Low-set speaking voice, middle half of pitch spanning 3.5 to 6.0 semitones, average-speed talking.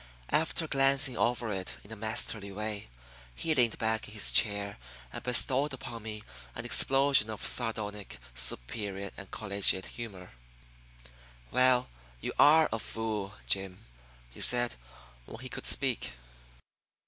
No: low, 110 Hz; average, 3.9 semitones; slow, 130 wpm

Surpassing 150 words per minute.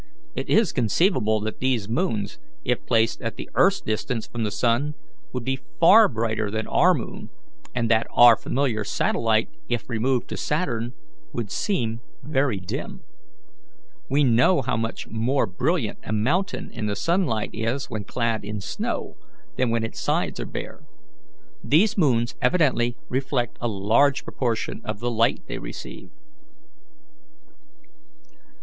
No: average, 145 wpm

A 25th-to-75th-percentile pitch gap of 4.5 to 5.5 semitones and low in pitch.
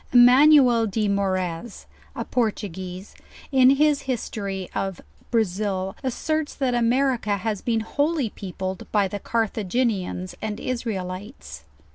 No: average, 4.8 semitones; high, 215 Hz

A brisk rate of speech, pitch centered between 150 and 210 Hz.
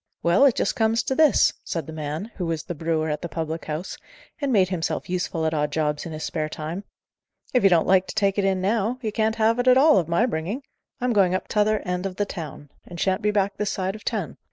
Yes: fast, 260 wpm; medium, 185 Hz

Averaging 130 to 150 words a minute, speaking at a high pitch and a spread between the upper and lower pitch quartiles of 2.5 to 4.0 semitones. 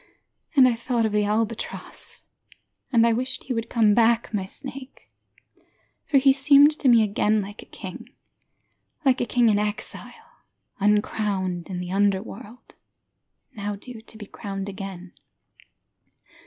Yes: average, 140 wpm; high, 220 Hz; average, 3.3 semitones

